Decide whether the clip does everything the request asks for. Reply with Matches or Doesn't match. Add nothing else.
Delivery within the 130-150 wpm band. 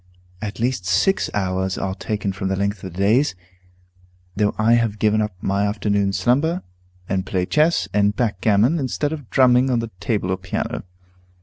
Doesn't match